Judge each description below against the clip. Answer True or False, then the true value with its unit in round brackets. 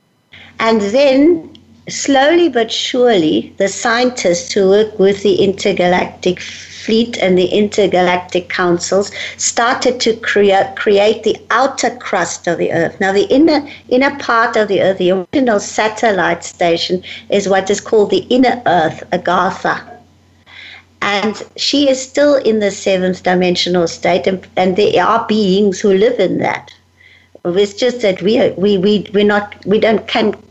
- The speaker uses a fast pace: False (150 wpm)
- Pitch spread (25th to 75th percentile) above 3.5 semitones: True (4.2 semitones)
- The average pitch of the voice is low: False (205 Hz)